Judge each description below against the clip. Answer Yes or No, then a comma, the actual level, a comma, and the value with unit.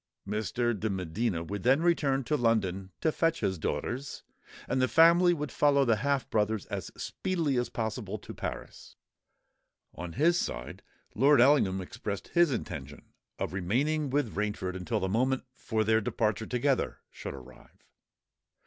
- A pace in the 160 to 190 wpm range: No, average, 150 wpm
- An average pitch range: No, wide, 6.3 semitones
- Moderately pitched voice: No, low, 115 Hz